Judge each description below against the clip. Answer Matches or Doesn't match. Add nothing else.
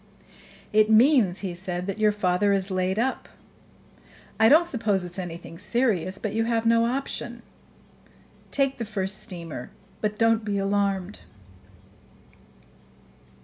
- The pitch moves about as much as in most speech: Matches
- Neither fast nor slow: Doesn't match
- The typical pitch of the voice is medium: Doesn't match